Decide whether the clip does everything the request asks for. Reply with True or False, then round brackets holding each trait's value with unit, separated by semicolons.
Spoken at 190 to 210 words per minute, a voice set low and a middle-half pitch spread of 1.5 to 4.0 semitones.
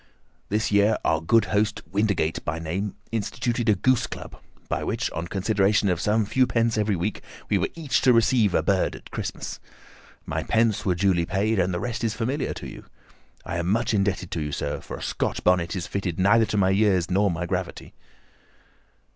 True (195 wpm; 100 Hz; 3.6 semitones)